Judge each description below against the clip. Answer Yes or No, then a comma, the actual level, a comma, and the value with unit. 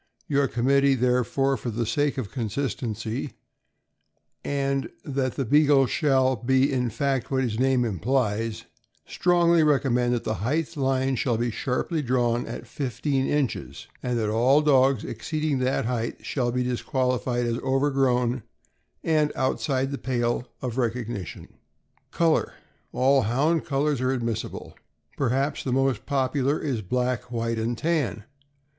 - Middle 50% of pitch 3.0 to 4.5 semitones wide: No, narrow, 2.6 semitones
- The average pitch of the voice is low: Yes, low, 130 Hz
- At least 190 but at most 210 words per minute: No, average, 140 wpm